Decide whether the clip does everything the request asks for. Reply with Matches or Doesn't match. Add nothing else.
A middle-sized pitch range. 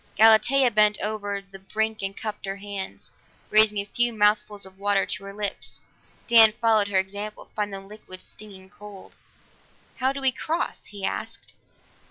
Doesn't match